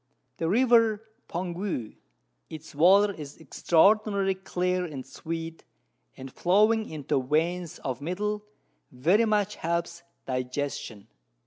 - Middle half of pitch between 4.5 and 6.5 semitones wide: Yes, average, 5.2 semitones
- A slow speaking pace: Yes, slow, 105 wpm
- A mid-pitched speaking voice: Yes, medium, 175 Hz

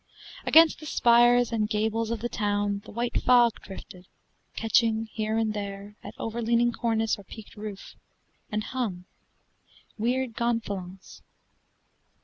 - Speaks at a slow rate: Yes, slow, 125 wpm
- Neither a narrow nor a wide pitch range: No, narrow, 2.3 semitones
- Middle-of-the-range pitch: No, high, 225 Hz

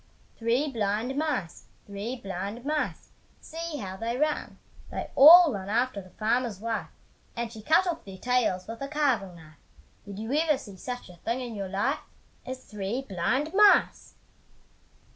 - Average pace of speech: Yes, average, 160 wpm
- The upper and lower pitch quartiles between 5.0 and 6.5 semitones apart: Yes, wide, 5.6 semitones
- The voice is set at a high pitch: Yes, high, 235 Hz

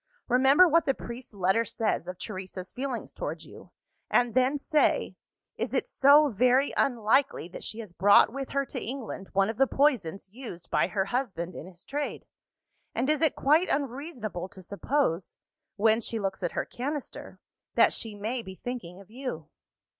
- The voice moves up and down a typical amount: No, wide, 5.9 semitones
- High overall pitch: Yes, high, 235 Hz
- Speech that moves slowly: No, average, 175 wpm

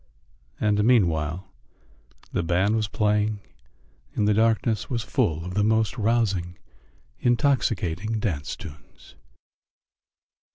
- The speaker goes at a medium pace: No, slow, 100 wpm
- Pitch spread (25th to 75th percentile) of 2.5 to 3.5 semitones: No, average, 4.0 semitones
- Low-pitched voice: Yes, low, 105 Hz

